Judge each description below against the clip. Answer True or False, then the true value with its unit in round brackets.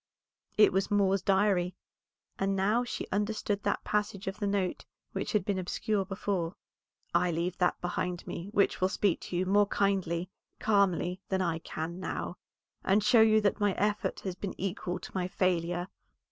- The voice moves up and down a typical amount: False (2.3 semitones)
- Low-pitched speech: False (190 Hz)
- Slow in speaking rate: False (175 wpm)